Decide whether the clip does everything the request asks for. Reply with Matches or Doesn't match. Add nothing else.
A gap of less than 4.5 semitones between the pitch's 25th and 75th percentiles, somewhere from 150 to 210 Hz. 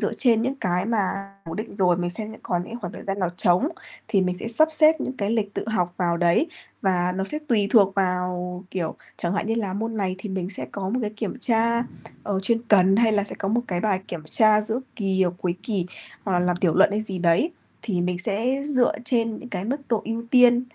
Matches